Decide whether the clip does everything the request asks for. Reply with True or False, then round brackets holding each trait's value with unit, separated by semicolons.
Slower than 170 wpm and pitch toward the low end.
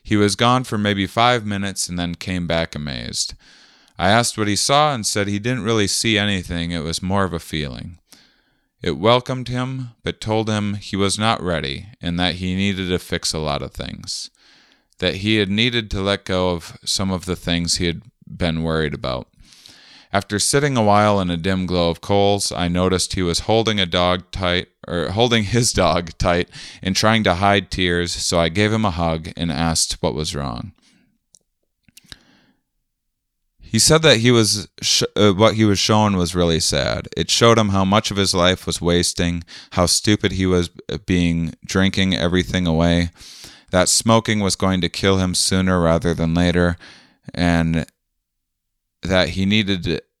False (185 wpm; 95 Hz)